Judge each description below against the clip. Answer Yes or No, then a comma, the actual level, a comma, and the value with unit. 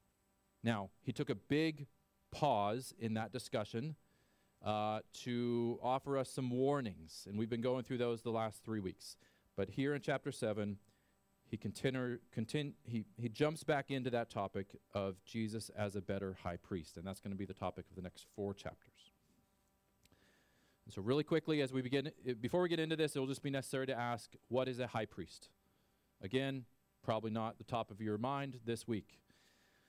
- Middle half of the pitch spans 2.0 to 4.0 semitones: No, average, 4.9 semitones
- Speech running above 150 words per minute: Yes, average, 185 wpm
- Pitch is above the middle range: No, low, 115 Hz